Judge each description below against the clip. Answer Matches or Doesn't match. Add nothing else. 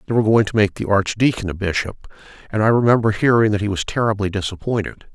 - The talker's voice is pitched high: Doesn't match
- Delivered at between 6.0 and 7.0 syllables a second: Matches